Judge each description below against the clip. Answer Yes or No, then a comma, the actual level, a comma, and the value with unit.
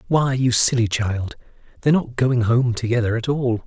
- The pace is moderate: Yes, average, 180 wpm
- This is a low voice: Yes, low, 120 Hz